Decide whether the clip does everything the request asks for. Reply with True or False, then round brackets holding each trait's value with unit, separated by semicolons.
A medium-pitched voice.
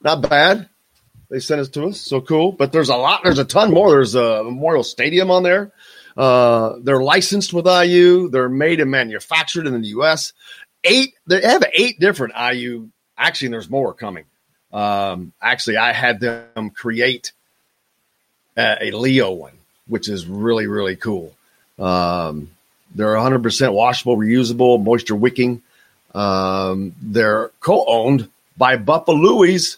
False (125 Hz)